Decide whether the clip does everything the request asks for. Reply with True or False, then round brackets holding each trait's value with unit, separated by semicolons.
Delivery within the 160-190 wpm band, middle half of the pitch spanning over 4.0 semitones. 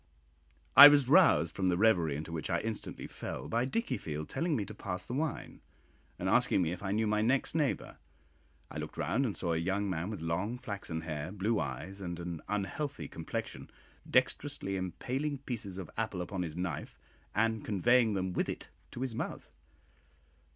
True (180 wpm; 5.3 semitones)